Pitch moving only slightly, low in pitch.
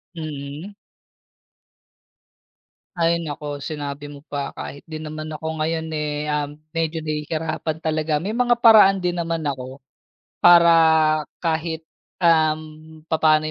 No: narrow, 1.7 semitones; medium, 155 Hz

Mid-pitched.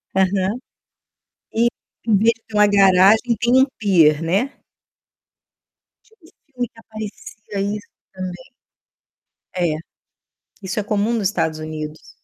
No: high, 205 Hz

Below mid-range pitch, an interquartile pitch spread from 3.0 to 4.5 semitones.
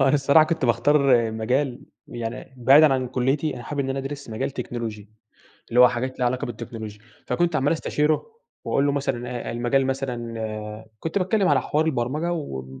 Yes: low, 130 Hz; average, 3.5 semitones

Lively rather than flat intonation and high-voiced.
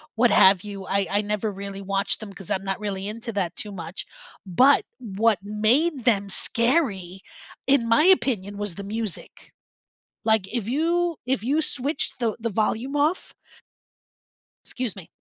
No: average, 4.2 semitones; high, 215 Hz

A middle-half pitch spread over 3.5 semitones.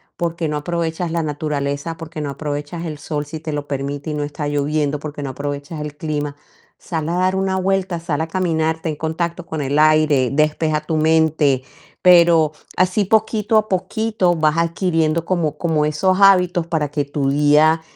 No: narrow, 2.6 semitones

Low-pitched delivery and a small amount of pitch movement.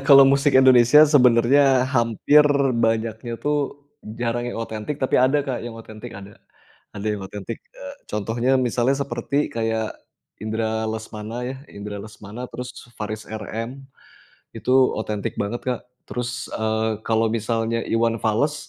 Yes: low, 115 Hz; narrow, 2.1 semitones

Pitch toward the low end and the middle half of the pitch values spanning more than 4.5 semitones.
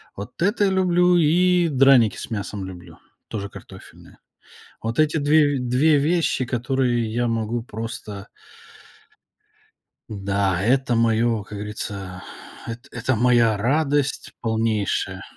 Yes: low, 120 Hz; average, 5.1 semitones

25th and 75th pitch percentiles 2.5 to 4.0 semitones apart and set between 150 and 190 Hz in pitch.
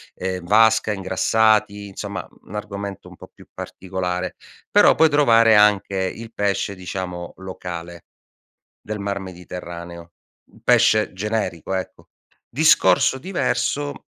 No: average, 2.9 semitones; low, 100 Hz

